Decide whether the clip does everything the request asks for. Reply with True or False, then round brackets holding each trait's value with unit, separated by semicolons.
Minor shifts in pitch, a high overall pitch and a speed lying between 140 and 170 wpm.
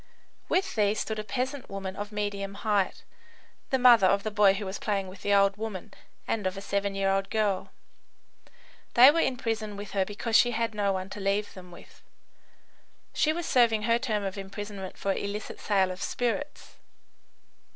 False (2.3 semitones; 205 Hz; 185 wpm)